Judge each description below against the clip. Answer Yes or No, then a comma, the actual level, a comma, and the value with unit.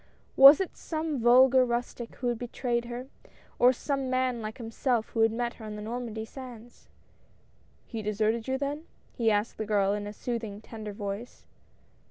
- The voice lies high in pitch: Yes, high, 235 Hz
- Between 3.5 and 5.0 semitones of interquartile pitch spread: No, average, 2.7 semitones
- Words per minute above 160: Yes, average, 175 wpm